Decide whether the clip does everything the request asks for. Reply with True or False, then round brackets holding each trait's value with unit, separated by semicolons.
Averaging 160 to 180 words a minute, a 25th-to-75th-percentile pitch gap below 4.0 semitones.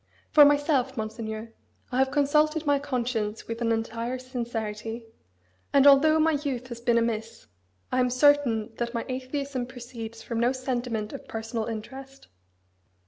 False (145 wpm; 3.2 semitones)